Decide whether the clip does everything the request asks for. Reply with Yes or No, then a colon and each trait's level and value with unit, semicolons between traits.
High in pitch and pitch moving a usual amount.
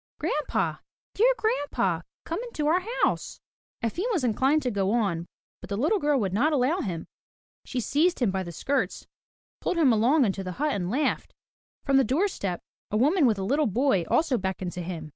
No: very high, 255 Hz; wide, 7.9 semitones